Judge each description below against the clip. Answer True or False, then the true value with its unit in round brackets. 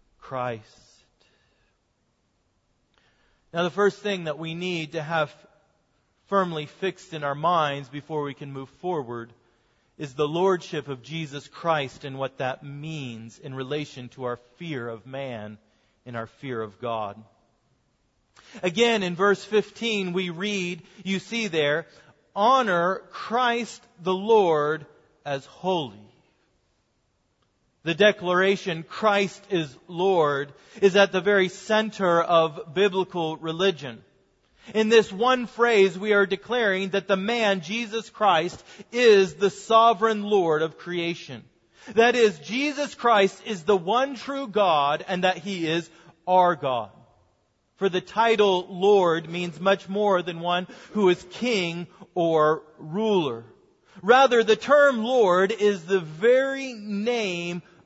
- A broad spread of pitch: True (5.7 semitones)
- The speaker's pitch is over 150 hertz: True (180 Hz)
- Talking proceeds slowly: True (130 wpm)